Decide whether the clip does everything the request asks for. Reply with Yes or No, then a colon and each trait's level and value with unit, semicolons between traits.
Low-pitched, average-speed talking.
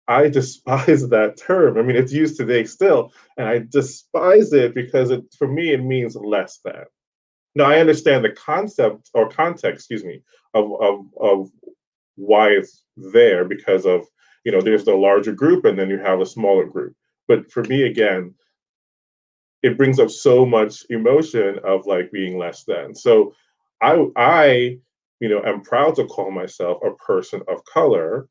No: medium, 145 Hz; average, 170 wpm